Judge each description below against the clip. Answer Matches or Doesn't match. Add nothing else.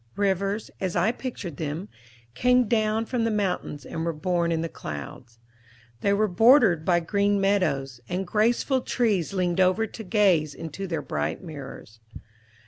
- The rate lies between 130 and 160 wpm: Matches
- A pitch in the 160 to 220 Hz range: Matches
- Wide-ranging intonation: Doesn't match